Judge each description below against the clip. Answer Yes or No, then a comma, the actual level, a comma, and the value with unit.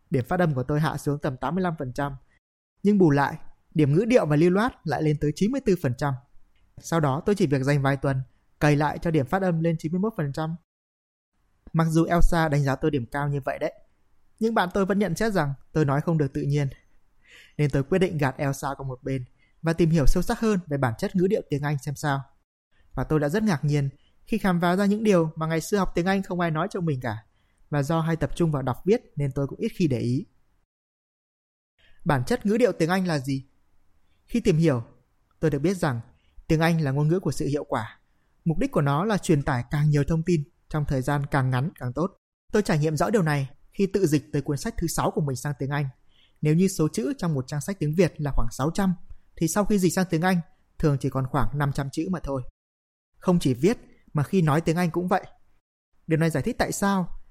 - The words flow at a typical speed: Yes, average, 240 wpm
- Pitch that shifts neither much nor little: Yes, average, 4.4 semitones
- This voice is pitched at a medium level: Yes, medium, 155 Hz